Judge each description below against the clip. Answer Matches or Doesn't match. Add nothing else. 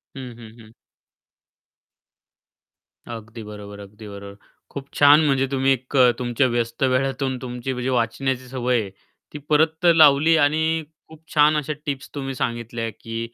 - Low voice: Matches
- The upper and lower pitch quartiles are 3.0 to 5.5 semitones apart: Matches